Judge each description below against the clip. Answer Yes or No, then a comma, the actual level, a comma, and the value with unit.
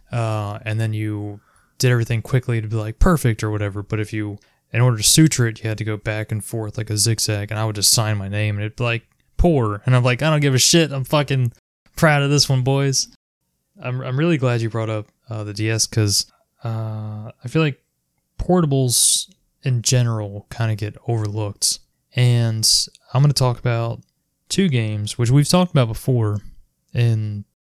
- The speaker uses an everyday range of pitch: Yes, average, 3.7 semitones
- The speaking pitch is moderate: No, low, 115 Hz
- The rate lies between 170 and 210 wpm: Yes, fast, 205 wpm